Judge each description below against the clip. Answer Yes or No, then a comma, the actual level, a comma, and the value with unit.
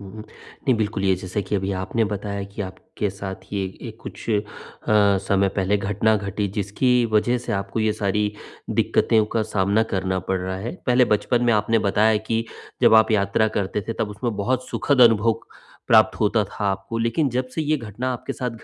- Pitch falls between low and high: No, low, 105 Hz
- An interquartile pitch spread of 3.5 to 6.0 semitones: No, narrow, 2.5 semitones